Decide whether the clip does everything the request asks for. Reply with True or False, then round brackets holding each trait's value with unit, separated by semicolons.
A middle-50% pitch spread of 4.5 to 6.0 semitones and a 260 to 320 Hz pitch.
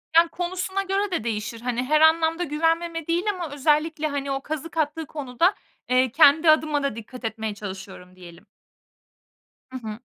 True (5.2 semitones; 300 Hz)